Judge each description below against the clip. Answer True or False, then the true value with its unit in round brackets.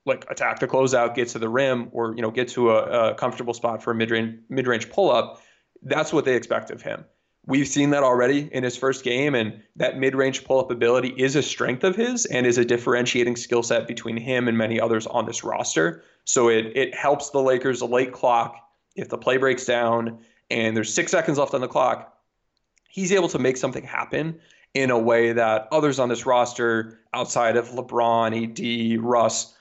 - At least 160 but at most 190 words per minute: False (205 wpm)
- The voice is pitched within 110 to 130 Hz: True (120 Hz)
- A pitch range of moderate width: False (2.3 semitones)